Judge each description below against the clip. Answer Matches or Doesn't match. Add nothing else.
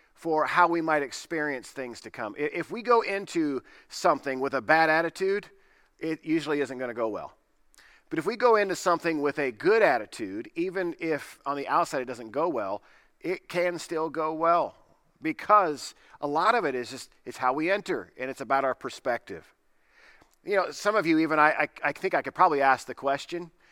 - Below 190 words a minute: Doesn't match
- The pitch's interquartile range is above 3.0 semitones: Matches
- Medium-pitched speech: Matches